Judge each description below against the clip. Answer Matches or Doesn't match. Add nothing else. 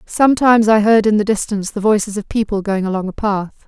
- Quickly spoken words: Matches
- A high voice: Matches